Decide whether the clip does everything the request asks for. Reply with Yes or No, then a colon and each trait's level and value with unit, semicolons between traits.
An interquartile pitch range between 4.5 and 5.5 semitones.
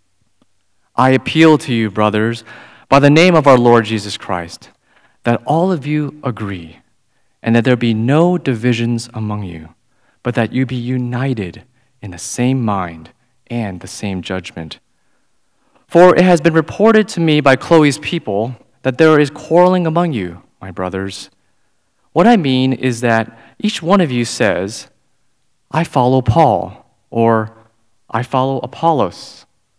Yes: average, 5.1 semitones